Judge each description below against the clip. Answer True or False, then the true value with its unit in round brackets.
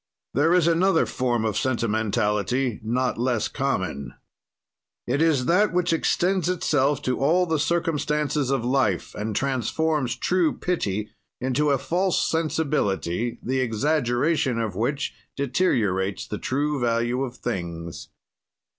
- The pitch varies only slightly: False (5.4 semitones)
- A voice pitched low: True (130 Hz)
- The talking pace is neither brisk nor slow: False (125 wpm)